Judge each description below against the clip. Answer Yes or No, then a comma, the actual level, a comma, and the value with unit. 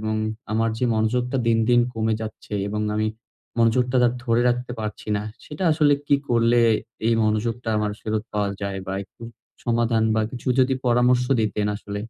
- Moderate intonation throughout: No, narrow, 2.2 semitones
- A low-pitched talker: Yes, low, 115 Hz